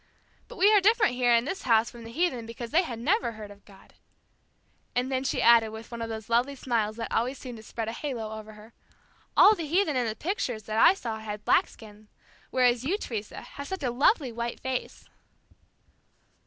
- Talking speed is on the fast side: Yes, fast, 210 wpm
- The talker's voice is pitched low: No, high, 235 Hz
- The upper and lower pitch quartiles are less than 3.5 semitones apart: No, average, 4.2 semitones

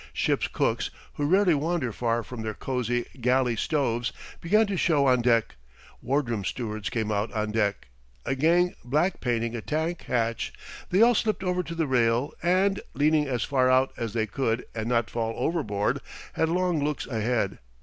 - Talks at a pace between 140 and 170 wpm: No, average, 180 wpm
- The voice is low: Yes, low, 130 Hz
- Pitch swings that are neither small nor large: No, wide, 5.9 semitones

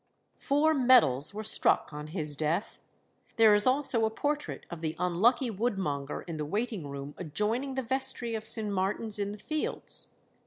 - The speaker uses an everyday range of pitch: No, wide, 7.3 semitones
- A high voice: Yes, high, 210 Hz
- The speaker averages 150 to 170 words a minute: Yes, average, 165 wpm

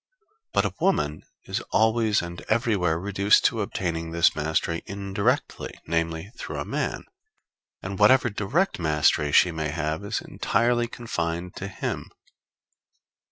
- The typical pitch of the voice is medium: No, very low, 95 Hz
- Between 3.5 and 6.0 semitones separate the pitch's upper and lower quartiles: Yes, average, 4.6 semitones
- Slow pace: Yes, slow, 130 wpm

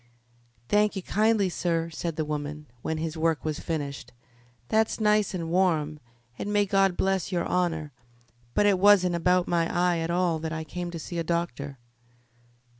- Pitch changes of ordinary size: Yes, average, 3.1 semitones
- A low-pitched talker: No, medium, 170 Hz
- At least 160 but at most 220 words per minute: Yes, average, 175 wpm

